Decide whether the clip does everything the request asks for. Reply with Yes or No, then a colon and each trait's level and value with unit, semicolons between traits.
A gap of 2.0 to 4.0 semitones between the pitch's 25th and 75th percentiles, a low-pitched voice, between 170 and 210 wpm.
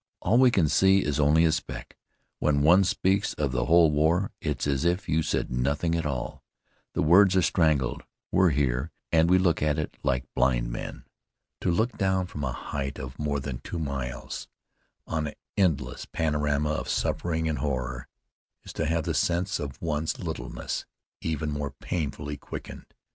Yes: average, 3.4 semitones; very low, 75 Hz; average, 175 wpm